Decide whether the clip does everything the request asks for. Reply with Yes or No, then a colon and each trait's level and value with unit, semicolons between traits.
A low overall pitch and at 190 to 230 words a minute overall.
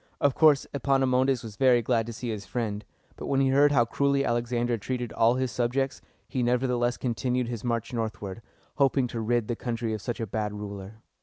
Yes: low, 120 Hz; average, 200 wpm